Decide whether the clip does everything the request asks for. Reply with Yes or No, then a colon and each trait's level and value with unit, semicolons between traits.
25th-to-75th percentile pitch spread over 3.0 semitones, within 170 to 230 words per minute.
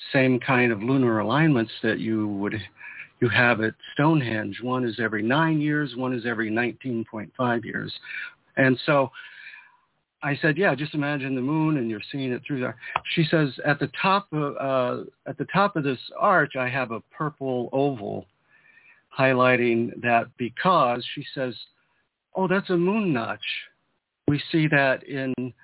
No: average, 3.7 semitones; average, 160 wpm